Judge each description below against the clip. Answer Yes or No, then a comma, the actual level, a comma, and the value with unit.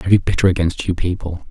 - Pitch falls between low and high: No, very low, 90 Hz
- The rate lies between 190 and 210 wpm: No, fast, 240 wpm